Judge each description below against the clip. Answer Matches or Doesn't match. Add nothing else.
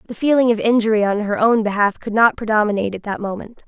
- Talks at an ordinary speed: Doesn't match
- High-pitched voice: Matches